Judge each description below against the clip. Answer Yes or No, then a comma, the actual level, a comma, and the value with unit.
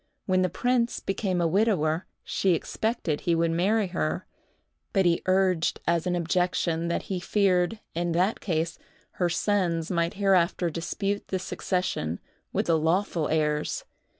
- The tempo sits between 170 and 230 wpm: No, average, 150 wpm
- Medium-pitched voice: Yes, medium, 175 Hz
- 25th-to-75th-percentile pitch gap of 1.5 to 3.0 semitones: Yes, narrow, 2.6 semitones